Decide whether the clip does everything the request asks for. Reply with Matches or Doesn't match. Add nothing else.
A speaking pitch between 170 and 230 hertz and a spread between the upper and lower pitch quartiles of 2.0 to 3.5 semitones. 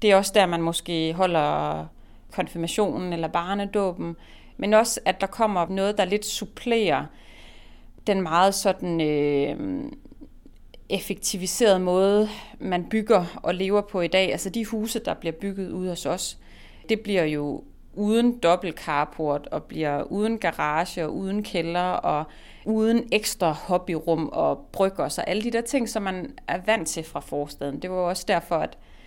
Doesn't match